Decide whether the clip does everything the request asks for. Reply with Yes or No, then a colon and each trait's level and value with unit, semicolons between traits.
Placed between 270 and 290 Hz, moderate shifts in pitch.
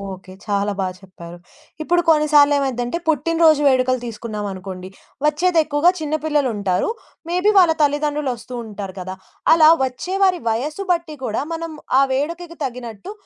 No: very high, 285 Hz; wide, 6.8 semitones